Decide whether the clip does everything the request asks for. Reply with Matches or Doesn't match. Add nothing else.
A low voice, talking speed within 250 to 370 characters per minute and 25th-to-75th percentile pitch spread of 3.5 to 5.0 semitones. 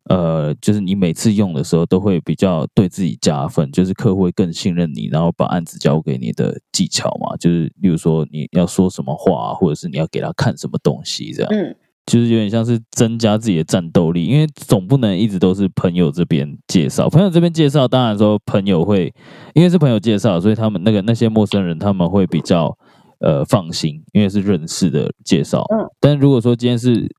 Doesn't match